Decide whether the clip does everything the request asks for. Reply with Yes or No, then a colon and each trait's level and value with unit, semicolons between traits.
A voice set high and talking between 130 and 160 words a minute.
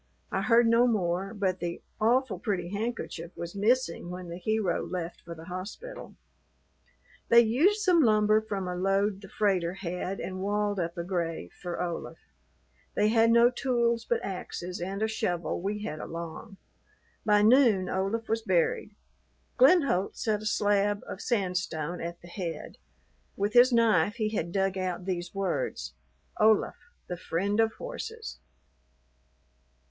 Yes: high, 200 Hz; average, 150 wpm